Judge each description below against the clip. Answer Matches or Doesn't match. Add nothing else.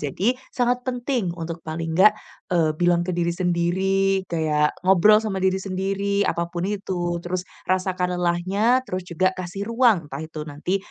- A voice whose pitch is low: Doesn't match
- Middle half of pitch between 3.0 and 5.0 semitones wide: Doesn't match